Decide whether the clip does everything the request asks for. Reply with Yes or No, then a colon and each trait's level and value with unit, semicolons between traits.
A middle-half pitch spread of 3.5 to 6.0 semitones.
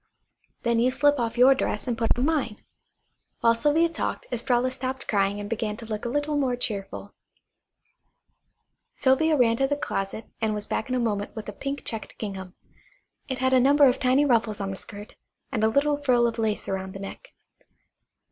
Yes: average, 4.0 semitones